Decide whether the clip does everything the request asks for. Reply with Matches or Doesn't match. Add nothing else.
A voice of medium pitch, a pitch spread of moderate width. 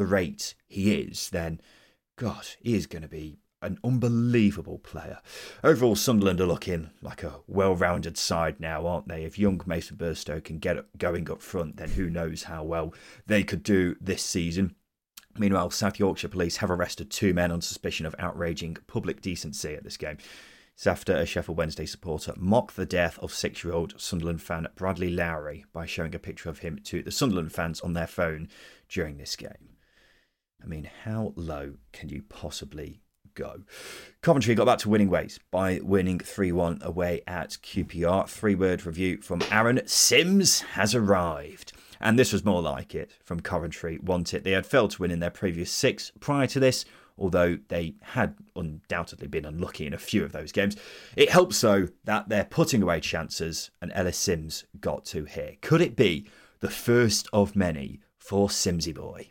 Doesn't match